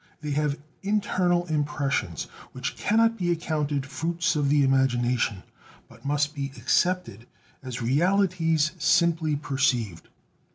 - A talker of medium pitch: Yes, medium, 150 Hz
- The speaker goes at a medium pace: No, slow, 115 wpm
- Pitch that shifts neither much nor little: Yes, average, 4.2 semitones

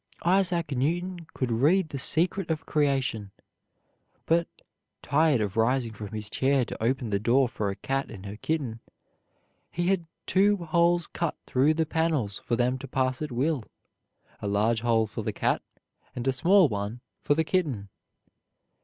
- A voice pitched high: No, low, 135 Hz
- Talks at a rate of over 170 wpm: No, average, 165 wpm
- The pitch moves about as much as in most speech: No, wide, 6.2 semitones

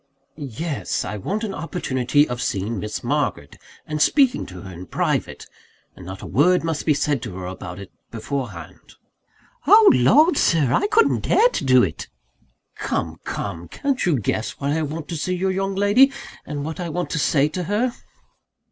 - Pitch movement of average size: No, wide, 8.5 semitones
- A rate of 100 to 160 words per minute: No, average, 185 wpm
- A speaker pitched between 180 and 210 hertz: No, medium, 150 Hz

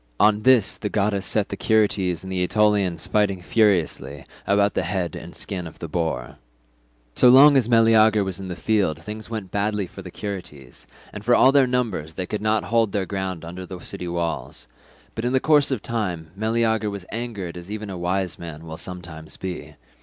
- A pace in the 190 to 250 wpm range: Yes, average, 200 wpm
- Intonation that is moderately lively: Yes, average, 3.7 semitones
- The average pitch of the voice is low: Yes, low, 100 Hz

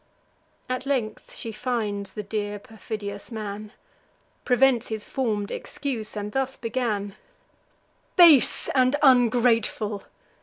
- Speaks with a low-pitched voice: No, high, 225 Hz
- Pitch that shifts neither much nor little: Yes, average, 3.5 semitones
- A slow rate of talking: Yes, slow, 105 wpm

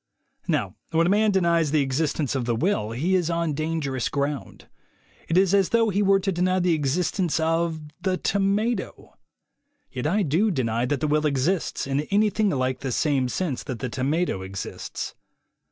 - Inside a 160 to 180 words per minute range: Yes, average, 175 wpm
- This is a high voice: No, medium, 160 Hz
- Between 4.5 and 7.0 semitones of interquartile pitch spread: Yes, wide, 5.5 semitones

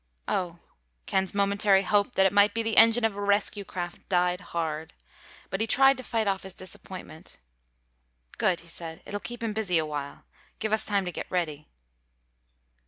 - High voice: Yes, high, 195 Hz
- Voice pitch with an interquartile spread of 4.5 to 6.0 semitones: No, average, 3.4 semitones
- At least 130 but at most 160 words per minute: No, average, 175 wpm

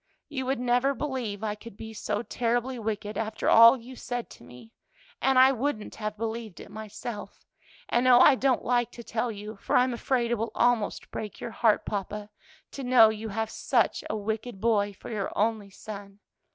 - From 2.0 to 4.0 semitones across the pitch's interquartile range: Yes, narrow, 2.6 semitones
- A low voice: No, high, 225 Hz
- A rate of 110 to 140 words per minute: No, average, 190 wpm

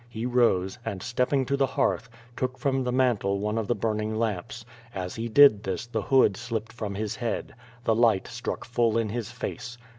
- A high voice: No, low, 115 Hz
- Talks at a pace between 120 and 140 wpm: No, fast, 205 wpm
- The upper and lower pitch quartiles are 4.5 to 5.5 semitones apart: No, average, 2.7 semitones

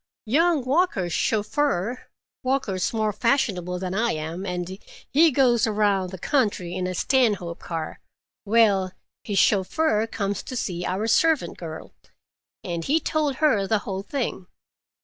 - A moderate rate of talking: No, slow, 130 wpm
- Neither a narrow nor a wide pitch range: No, wide, 5.9 semitones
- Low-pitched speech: No, high, 210 Hz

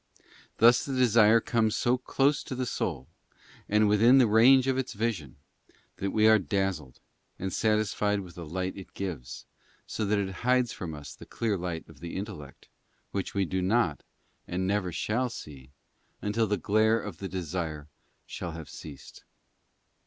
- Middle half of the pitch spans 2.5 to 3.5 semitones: No, average, 4.4 semitones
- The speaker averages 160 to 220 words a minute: Yes, average, 165 wpm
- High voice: No, low, 100 Hz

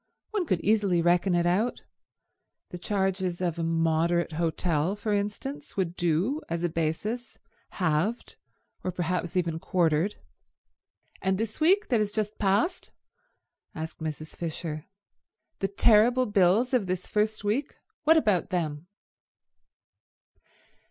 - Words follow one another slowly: Yes, slow, 125 wpm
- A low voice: No, medium, 185 Hz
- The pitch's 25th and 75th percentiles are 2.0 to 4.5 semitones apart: Yes, average, 4.1 semitones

